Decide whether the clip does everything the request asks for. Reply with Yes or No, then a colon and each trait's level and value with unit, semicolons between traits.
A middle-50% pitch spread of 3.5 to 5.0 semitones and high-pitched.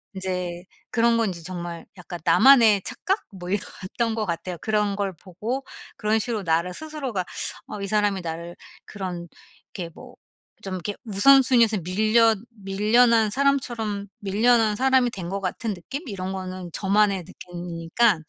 Yes: average, 3.9 semitones; high, 205 Hz